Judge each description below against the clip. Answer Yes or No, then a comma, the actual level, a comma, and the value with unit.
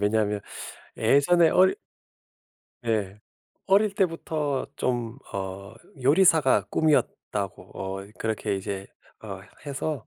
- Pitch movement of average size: No, wide, 7.8 semitones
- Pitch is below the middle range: Yes, low, 120 Hz